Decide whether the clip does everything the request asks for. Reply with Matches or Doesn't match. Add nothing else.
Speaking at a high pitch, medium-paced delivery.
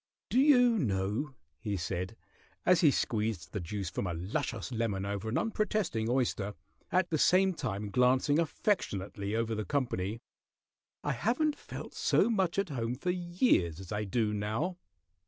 Doesn't match